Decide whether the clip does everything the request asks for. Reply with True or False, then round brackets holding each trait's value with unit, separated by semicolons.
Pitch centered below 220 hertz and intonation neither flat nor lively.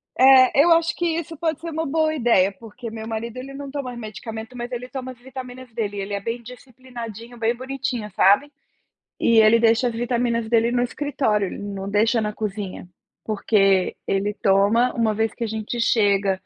False (235 Hz; 3.2 semitones)